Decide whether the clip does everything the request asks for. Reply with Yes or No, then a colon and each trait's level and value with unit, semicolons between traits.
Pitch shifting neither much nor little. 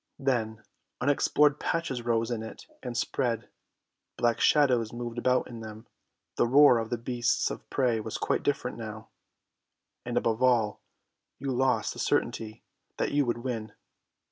No: narrow, 2.3 semitones